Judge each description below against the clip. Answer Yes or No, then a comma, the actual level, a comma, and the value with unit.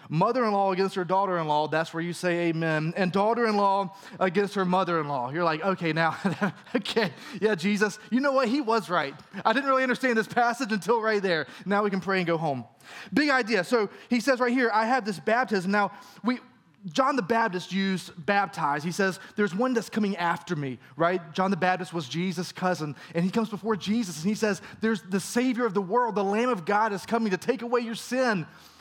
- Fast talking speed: Yes, fast, 210 wpm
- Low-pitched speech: No, high, 200 Hz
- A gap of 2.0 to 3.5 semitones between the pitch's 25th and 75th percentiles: No, average, 4.5 semitones